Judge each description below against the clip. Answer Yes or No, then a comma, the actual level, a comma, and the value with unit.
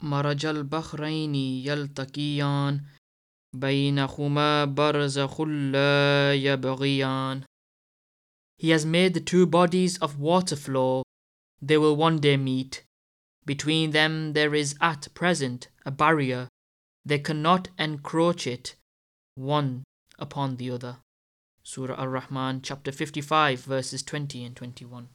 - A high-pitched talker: No, medium, 140 Hz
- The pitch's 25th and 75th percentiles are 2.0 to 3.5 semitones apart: Yes, average, 2.8 semitones